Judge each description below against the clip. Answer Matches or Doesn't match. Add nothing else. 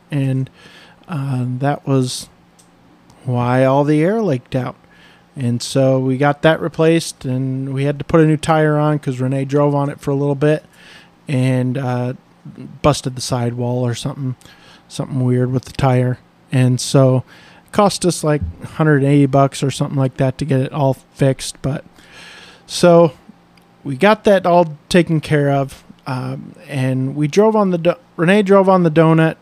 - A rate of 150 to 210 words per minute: Matches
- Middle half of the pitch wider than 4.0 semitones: Doesn't match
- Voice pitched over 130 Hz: Matches